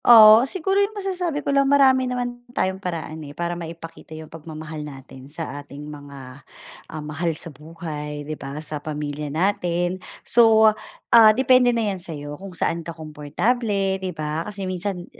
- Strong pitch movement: Yes, wide, 6.7 semitones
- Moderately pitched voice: Yes, medium, 170 Hz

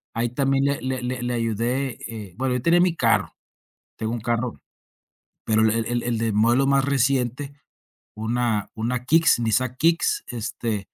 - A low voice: Yes, low, 120 Hz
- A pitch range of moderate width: Yes, average, 3.0 semitones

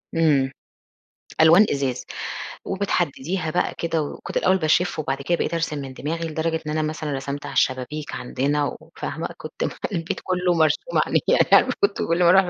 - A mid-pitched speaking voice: Yes, medium, 160 Hz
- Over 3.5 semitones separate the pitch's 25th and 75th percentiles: No, average, 3.1 semitones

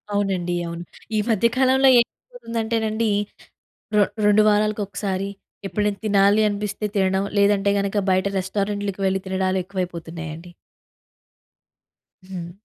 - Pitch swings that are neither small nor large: No, narrow, 2.0 semitones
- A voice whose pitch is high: Yes, high, 200 Hz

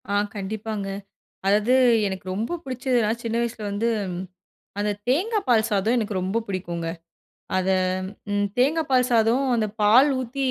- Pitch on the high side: Yes, high, 220 Hz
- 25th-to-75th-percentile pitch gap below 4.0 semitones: Yes, average, 3.6 semitones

